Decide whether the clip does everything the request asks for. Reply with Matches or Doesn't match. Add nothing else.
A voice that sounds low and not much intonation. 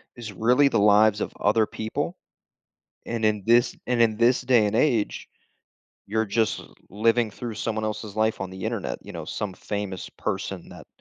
Matches